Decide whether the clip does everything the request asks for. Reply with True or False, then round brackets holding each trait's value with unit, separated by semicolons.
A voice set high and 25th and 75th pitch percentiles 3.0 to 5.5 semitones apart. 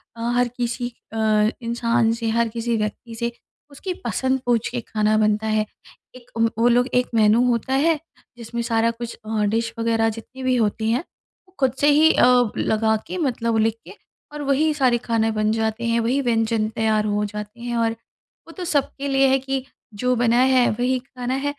False (235 Hz; 2.5 semitones)